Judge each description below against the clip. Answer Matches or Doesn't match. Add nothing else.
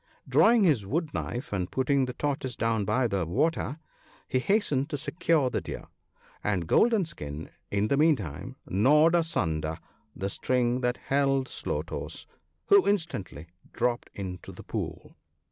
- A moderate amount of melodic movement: Doesn't match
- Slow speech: Doesn't match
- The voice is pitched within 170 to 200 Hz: Doesn't match